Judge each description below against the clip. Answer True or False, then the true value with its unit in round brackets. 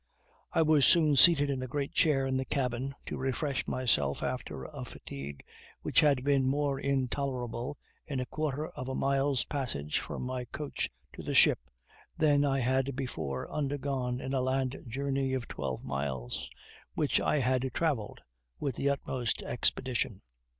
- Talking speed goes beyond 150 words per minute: True (160 wpm)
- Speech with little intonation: True (2.1 semitones)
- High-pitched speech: False (130 Hz)